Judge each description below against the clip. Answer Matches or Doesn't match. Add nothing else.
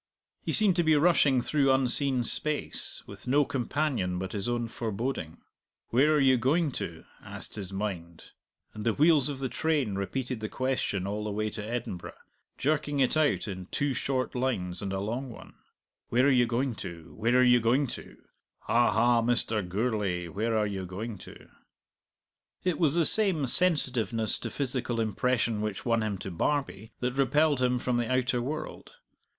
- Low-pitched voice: Matches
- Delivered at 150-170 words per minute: Doesn't match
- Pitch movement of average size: Matches